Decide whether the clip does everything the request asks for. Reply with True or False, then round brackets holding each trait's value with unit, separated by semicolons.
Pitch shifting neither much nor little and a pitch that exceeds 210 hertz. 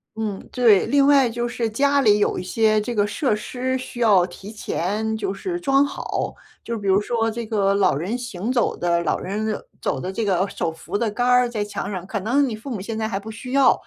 True (3.5 semitones; 220 Hz)